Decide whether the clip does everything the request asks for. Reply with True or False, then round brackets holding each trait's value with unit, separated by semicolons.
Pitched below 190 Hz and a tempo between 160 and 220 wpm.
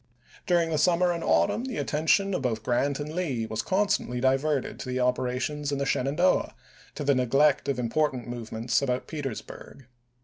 True (140 Hz; 170 wpm)